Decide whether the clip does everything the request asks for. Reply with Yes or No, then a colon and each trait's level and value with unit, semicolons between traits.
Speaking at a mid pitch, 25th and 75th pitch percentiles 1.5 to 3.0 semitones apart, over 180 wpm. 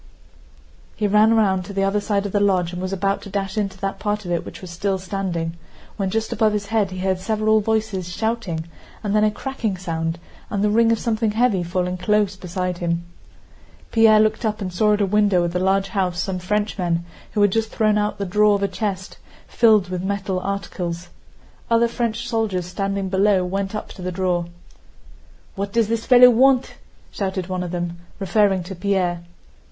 No: high, 195 Hz; narrow, 2.6 semitones; average, 200 wpm